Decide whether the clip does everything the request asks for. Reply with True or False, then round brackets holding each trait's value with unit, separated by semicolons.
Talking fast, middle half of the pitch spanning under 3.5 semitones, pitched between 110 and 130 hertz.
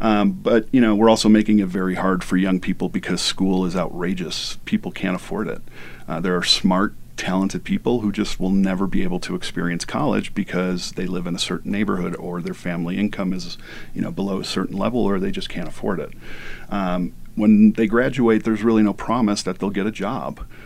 False (210 wpm; 3.1 semitones; 95 Hz)